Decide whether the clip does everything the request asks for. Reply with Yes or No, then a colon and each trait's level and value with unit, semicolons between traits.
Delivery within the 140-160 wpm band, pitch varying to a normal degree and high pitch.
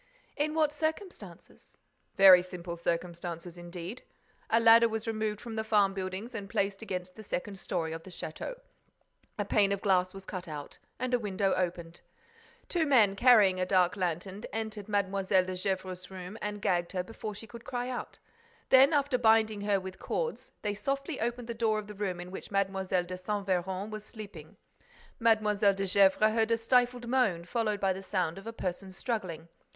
No: average, 185 wpm; average, 3.5 semitones; high, 200 Hz